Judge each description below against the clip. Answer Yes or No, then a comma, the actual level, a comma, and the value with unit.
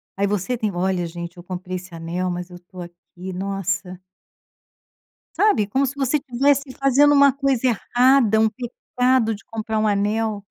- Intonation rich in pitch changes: Yes, wide, 5.8 semitones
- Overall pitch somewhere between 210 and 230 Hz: Yes, high, 215 Hz